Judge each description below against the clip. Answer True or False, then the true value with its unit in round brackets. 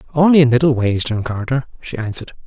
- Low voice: True (130 Hz)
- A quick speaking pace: False (195 wpm)